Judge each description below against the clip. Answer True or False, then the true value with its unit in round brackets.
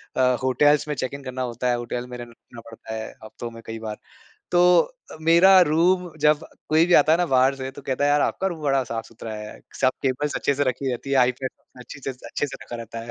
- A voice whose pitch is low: True (130 Hz)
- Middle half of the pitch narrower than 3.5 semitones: False (3.8 semitones)